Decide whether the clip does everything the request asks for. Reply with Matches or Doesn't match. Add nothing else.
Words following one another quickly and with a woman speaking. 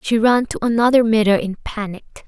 Doesn't match